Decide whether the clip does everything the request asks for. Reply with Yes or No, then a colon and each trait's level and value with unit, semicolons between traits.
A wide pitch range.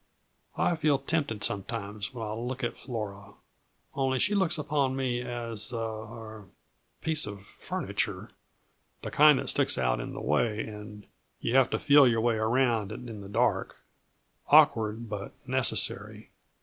No: average, 3.9 semitones